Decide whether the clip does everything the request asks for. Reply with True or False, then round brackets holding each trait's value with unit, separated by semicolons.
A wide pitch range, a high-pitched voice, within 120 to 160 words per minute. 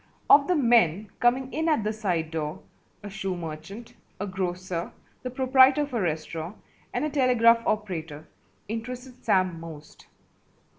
True (6.8 semitones; 210 Hz; 145 wpm)